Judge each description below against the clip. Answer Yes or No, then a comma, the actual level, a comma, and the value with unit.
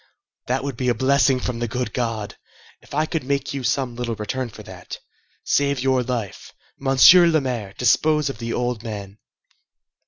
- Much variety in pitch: No, average, 2.8 semitones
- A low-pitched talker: Yes, low, 125 Hz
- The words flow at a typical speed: Yes, average, 180 wpm